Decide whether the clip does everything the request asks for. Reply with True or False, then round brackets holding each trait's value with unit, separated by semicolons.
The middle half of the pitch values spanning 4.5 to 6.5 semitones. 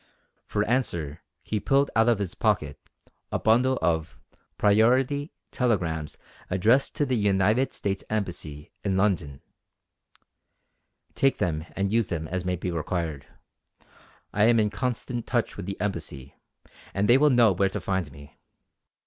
True (5.6 semitones)